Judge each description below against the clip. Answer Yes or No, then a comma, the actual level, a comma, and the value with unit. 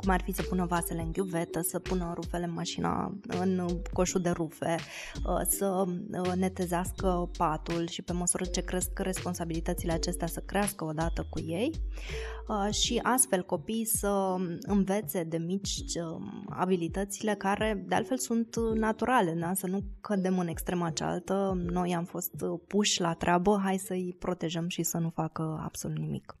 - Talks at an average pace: Yes, average, 150 wpm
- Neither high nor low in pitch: Yes, medium, 180 Hz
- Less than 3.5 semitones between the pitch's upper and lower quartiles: Yes, narrow, 2.4 semitones